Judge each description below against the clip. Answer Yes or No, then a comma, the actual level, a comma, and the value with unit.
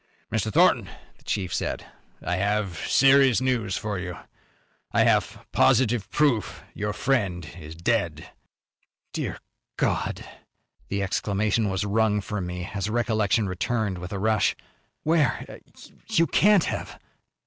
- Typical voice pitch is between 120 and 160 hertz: No, low, 105 Hz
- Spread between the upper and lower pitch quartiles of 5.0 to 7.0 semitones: No, average, 3.9 semitones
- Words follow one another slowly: Yes, slow, 125 wpm